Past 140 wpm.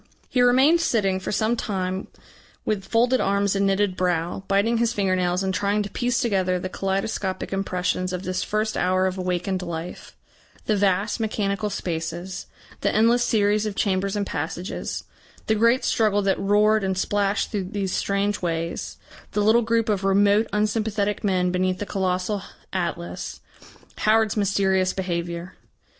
Yes: average, 155 wpm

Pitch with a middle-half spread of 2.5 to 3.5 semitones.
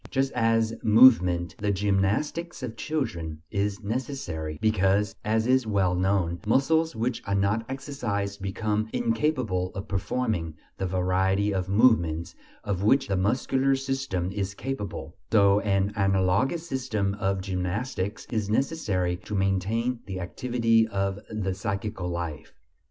No: average, 4.2 semitones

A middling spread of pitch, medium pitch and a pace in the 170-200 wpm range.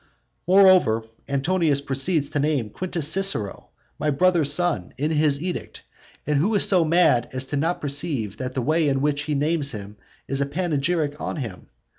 Yes: average, 3.7 semitones; medium, 145 Hz; average, 175 wpm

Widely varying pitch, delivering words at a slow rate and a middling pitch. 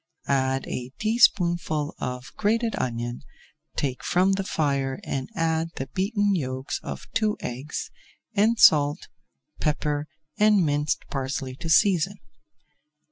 Yes: wide, 6.6 semitones; slow, 120 wpm; medium, 150 Hz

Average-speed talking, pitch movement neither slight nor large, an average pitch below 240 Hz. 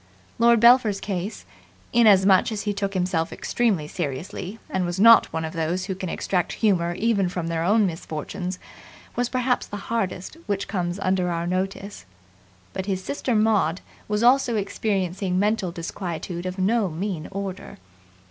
Yes: average, 155 wpm; average, 3.1 semitones; high, 190 Hz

